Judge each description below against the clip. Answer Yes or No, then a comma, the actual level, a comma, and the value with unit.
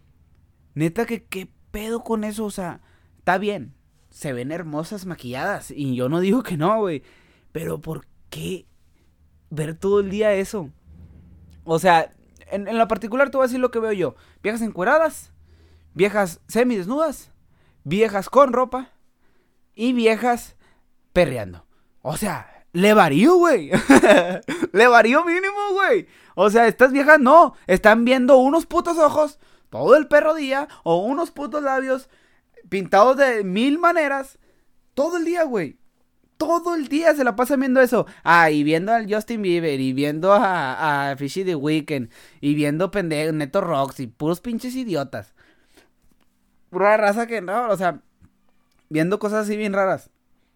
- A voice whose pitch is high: Yes, high, 205 Hz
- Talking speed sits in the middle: Yes, average, 155 wpm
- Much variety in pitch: Yes, wide, 8.9 semitones